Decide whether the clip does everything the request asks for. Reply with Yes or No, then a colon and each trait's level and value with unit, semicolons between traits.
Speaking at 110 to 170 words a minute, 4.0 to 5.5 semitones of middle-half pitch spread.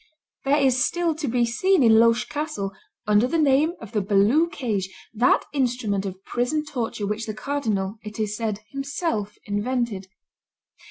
Yes: average, 160 wpm; average, 5.1 semitones